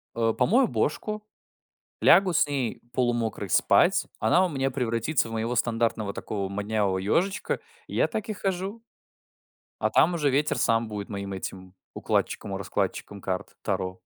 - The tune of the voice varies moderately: No, wide, 7.8 semitones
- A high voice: No, low, 115 Hz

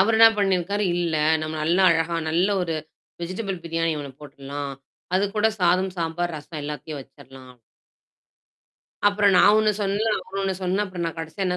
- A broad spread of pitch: No, average, 3.8 semitones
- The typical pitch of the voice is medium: Yes, medium, 175 Hz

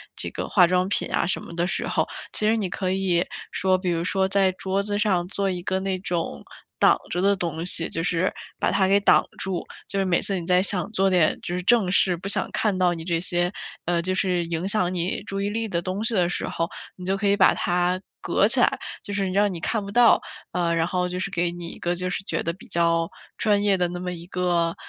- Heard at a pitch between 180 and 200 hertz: Yes, medium, 185 Hz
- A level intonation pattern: Yes, narrow, 2.1 semitones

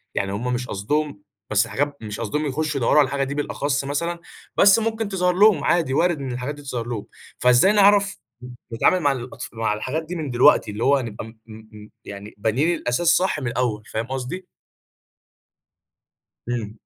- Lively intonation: Yes, wide, 5.9 semitones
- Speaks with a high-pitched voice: No, low, 135 Hz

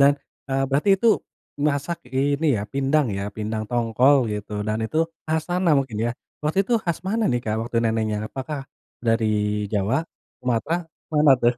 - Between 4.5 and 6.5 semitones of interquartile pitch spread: Yes, average, 5.3 semitones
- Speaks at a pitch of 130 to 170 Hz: Yes, low, 135 Hz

